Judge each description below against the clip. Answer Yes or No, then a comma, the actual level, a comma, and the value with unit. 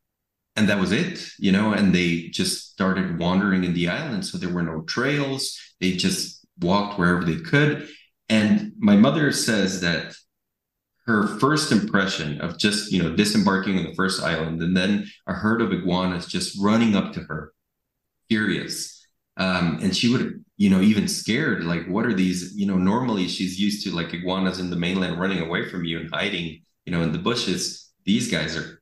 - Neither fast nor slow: Yes, average, 190 wpm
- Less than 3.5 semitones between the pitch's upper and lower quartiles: No, average, 4.5 semitones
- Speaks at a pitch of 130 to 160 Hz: No, very low, 95 Hz